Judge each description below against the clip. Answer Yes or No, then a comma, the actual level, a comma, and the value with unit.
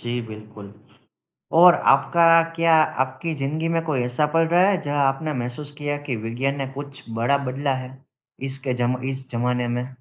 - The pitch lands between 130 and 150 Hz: Yes, low, 135 Hz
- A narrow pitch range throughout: No, average, 3.3 semitones